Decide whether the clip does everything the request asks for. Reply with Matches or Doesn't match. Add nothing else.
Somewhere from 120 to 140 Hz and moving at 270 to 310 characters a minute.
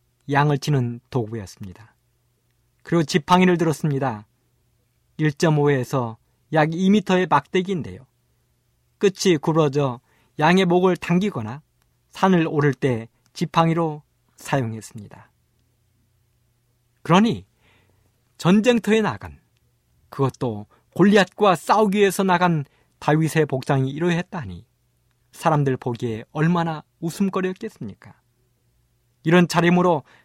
Doesn't match